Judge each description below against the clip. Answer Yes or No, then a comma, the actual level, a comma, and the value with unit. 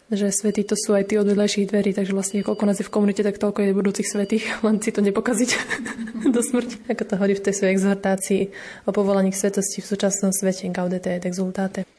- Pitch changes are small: Yes, narrow, 1.5 semitones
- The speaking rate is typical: No, fast, 215 wpm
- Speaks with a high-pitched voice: Yes, high, 205 Hz